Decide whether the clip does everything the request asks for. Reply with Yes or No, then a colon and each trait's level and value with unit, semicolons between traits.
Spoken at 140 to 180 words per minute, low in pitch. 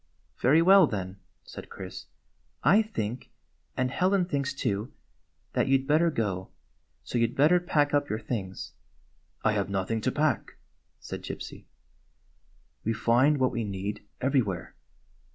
Yes: average, 165 wpm; low, 125 Hz